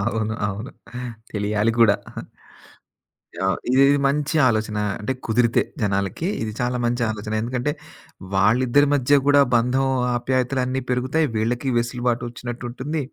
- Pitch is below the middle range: Yes, low, 120 Hz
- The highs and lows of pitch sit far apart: No, average, 3.2 semitones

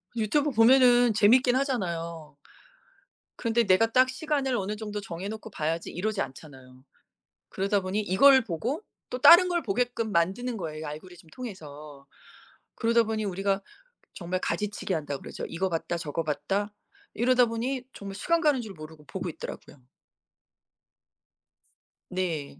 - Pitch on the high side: Yes, high, 205 Hz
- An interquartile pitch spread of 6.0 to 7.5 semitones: Yes, wide, 6.5 semitones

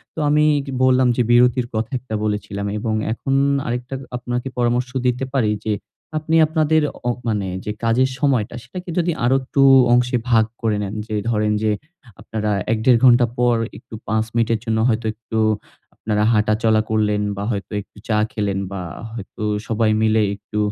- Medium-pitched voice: No, low, 115 Hz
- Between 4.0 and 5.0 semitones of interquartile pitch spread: No, average, 2.7 semitones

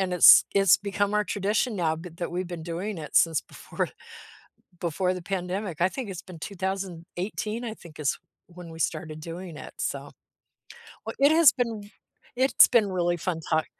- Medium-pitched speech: Yes, medium, 180 Hz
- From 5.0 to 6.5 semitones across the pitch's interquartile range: No, average, 3.2 semitones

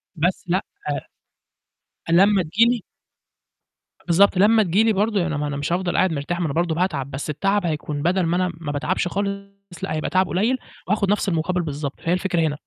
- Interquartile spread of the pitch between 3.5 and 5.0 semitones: Yes, average, 4.0 semitones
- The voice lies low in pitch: No, medium, 175 Hz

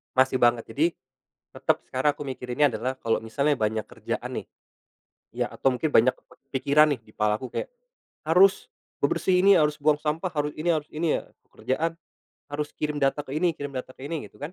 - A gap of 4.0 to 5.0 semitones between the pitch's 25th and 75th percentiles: No, average, 3.2 semitones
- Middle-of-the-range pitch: Yes, medium, 145 Hz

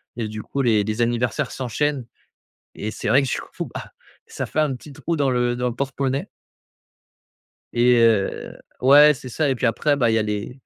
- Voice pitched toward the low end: Yes, low, 125 Hz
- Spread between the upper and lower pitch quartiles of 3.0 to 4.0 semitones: Yes, average, 3.3 semitones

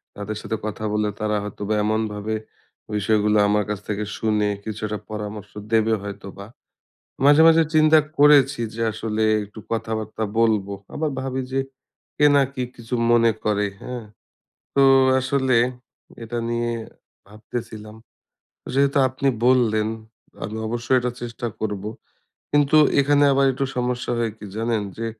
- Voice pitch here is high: No, low, 110 Hz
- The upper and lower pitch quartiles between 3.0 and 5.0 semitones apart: Yes, average, 3.4 semitones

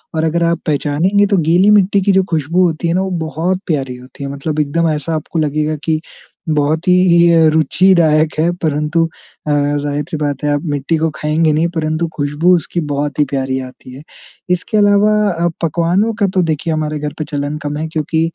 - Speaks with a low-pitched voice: No, medium, 155 Hz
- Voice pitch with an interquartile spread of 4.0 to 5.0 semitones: No, narrow, 2.5 semitones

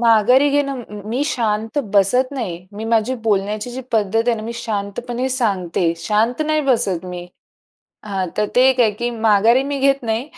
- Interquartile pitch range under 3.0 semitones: No, average, 3.5 semitones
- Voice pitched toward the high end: Yes, high, 225 Hz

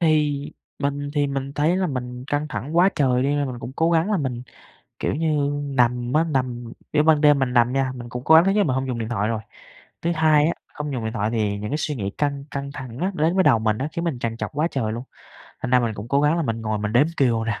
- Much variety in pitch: No, average, 3.9 semitones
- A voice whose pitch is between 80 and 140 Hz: Yes, low, 135 Hz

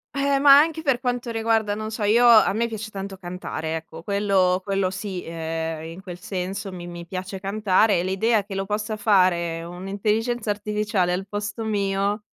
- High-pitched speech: Yes, high, 200 Hz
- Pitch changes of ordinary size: Yes, average, 3.0 semitones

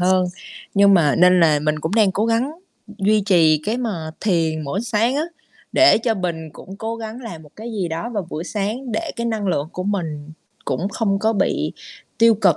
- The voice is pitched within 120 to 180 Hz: No, high, 195 Hz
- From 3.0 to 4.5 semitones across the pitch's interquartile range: No, average, 5.1 semitones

